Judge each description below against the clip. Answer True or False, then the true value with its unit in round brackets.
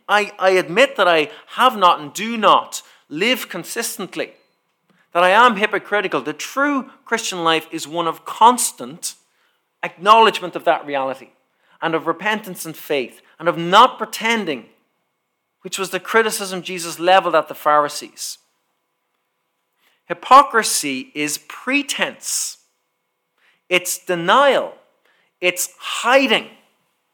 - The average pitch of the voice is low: False (185 Hz)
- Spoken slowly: True (115 wpm)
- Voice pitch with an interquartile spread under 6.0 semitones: True (5.3 semitones)